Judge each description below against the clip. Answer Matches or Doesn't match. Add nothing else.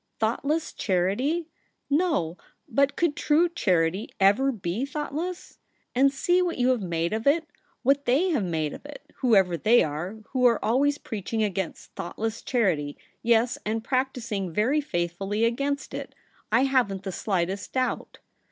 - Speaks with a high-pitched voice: Matches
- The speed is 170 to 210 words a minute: Doesn't match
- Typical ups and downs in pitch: Doesn't match